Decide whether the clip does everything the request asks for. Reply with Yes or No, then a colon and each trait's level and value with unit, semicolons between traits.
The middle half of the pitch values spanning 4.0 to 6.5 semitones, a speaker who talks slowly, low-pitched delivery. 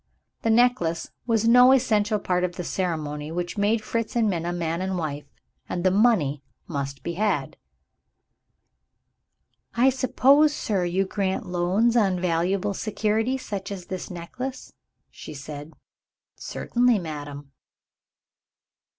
No: average, 5.0 semitones; slow, 125 wpm; high, 190 Hz